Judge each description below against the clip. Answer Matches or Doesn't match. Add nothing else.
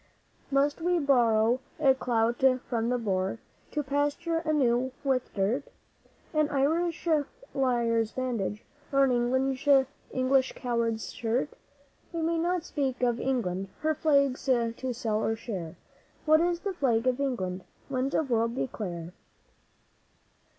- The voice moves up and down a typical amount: Matches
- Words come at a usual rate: Doesn't match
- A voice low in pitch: Doesn't match